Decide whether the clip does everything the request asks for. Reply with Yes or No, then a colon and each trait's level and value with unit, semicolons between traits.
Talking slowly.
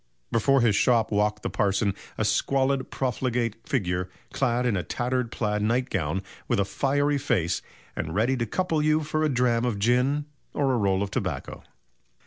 No: average, 165 wpm